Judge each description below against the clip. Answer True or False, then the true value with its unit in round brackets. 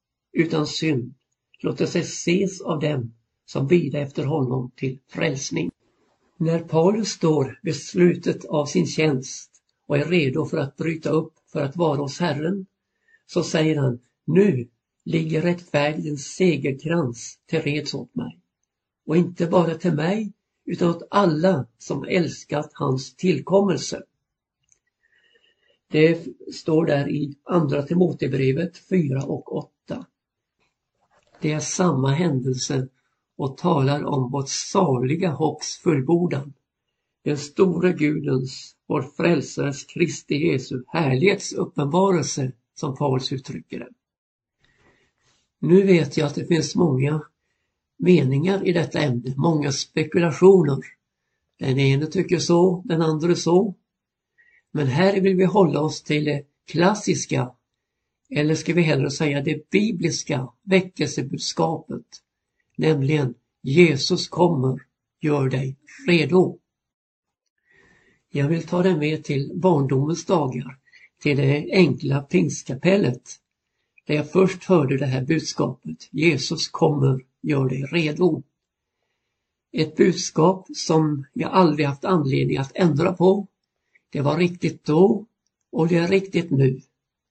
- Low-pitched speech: False (155 Hz)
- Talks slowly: True (120 wpm)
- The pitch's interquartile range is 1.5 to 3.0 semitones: False (4.0 semitones)